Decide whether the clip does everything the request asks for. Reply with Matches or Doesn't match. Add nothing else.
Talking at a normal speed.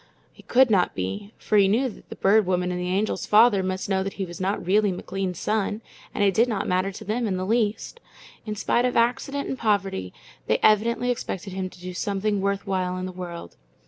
Doesn't match